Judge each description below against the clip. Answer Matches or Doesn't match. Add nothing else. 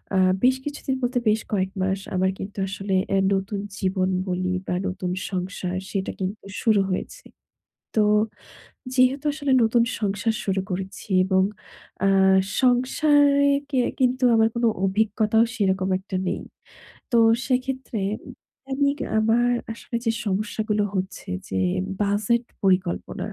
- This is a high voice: Matches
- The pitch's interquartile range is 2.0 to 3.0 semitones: Doesn't match